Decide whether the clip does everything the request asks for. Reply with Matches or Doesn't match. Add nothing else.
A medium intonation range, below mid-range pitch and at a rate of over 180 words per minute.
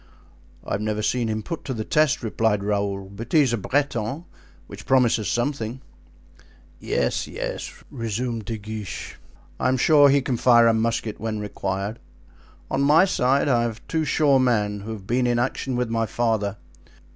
Doesn't match